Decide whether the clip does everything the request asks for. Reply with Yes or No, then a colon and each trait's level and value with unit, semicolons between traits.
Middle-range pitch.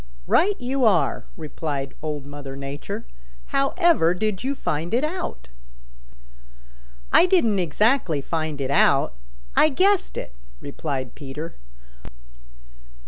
Yes: medium, 165 Hz